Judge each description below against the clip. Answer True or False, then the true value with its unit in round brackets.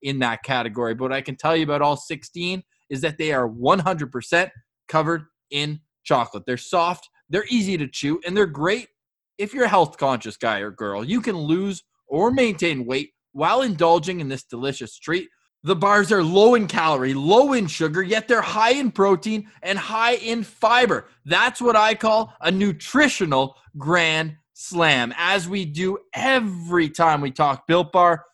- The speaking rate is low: False (180 wpm)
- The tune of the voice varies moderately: False (6.7 semitones)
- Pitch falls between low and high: True (170 Hz)